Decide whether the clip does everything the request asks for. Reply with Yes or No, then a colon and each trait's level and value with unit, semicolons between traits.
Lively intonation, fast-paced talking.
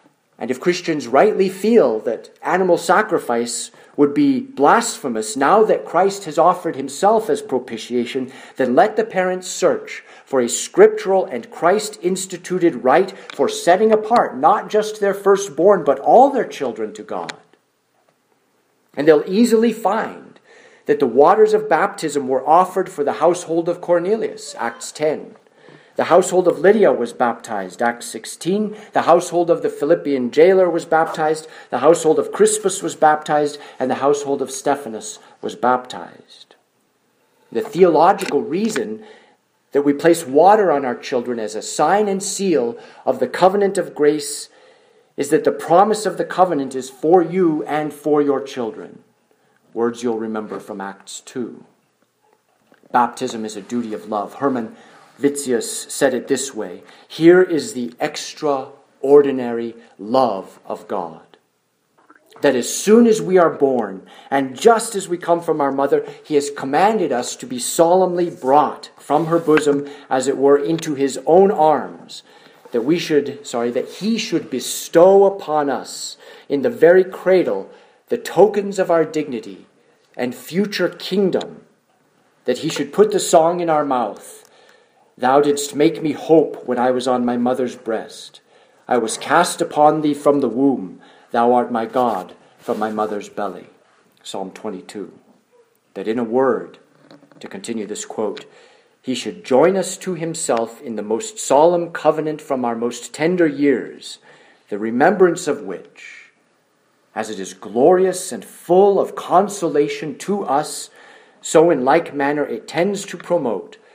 No: wide, 6.4 semitones; average, 150 wpm